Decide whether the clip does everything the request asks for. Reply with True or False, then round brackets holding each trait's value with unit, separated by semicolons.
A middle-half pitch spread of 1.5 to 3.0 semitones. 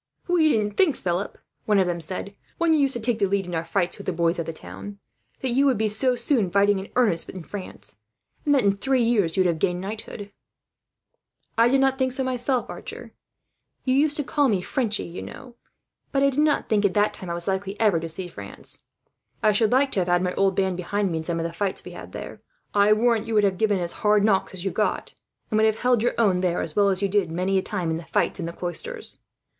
False (5.0 semitones)